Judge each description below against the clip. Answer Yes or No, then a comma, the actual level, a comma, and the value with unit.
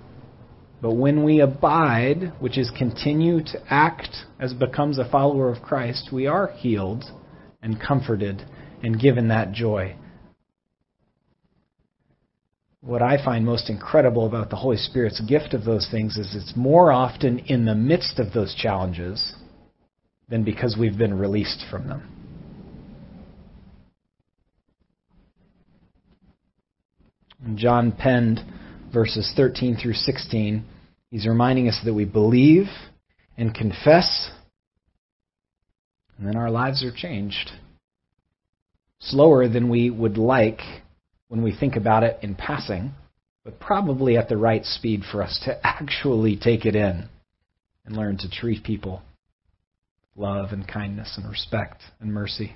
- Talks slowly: Yes, slow, 130 wpm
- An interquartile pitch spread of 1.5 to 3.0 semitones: No, average, 3.7 semitones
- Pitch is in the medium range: No, low, 115 Hz